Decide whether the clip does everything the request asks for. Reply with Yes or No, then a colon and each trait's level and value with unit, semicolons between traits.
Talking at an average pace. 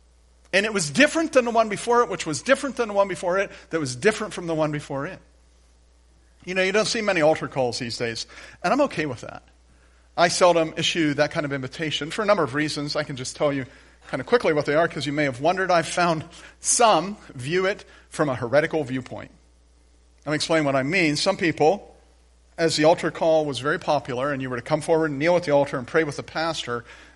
No: fast, 240 wpm